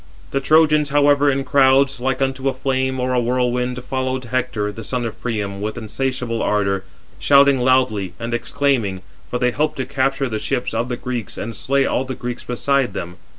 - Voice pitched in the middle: No, low, 125 Hz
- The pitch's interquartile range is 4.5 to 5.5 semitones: No, narrow, 2.6 semitones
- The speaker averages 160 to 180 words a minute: No, average, 190 wpm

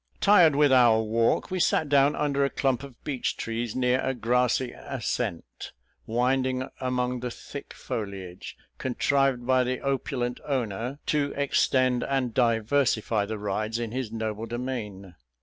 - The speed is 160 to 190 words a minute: No, average, 145 wpm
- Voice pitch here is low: Yes, low, 125 Hz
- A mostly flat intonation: No, average, 3.0 semitones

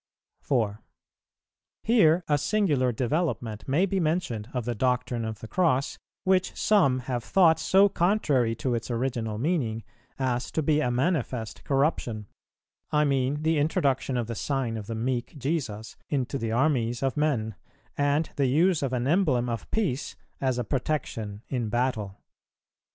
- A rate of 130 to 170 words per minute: Yes, average, 155 wpm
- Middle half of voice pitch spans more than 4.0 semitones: Yes, average, 4.7 semitones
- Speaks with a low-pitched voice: Yes, low, 130 Hz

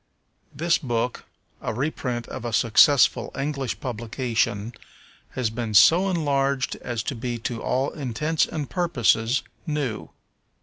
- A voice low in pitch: Yes, low, 125 Hz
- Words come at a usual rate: No, slow, 125 wpm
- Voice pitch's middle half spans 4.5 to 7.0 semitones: No, average, 3.8 semitones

